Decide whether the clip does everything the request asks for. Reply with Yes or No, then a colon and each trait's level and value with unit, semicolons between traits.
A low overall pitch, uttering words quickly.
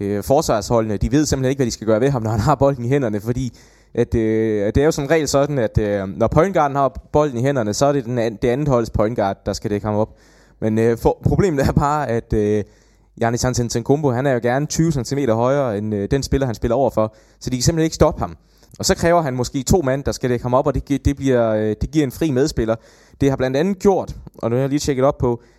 Yes: low, 125 Hz; fast, 270 wpm